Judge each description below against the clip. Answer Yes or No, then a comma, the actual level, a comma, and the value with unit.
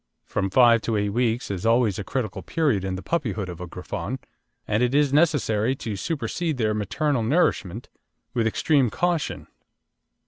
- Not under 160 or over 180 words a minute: Yes, average, 165 wpm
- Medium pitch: No, low, 115 Hz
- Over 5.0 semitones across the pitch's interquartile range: Yes, wide, 5.5 semitones